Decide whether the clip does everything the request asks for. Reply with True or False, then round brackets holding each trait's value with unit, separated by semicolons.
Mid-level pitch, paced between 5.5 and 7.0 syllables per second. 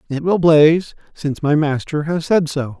False (155 Hz; 5.0 syllables/s)